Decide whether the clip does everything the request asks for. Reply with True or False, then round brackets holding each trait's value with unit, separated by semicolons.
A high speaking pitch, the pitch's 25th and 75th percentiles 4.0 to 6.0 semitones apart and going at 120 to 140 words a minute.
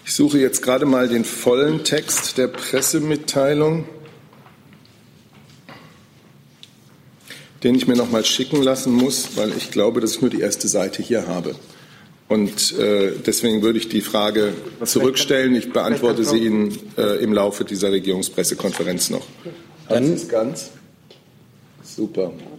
False (125 Hz; 4.6 semitones; 130 wpm)